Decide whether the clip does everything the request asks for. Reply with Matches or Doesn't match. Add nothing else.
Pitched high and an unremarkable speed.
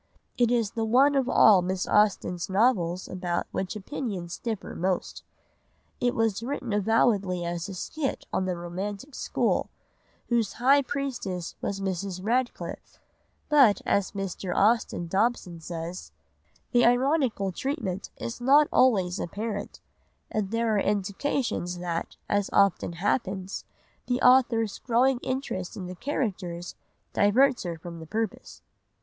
Doesn't match